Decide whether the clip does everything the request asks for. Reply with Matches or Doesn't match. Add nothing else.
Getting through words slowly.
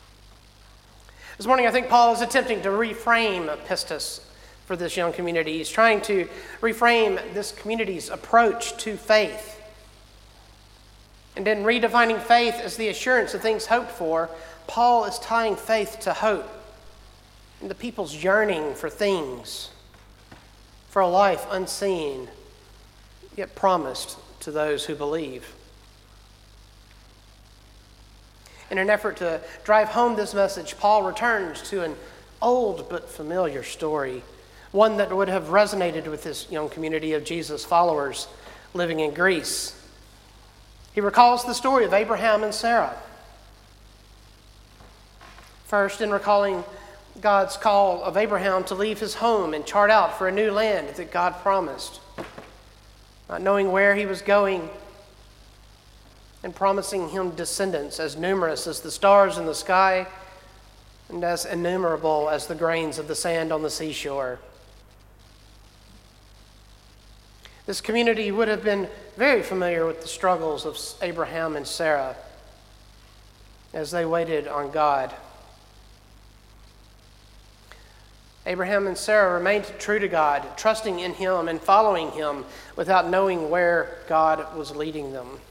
Matches